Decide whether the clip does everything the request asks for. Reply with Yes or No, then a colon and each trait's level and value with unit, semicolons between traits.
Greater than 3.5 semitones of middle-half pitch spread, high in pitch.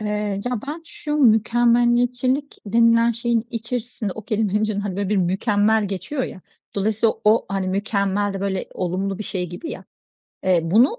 No: average, 3.2 semitones; high, 215 Hz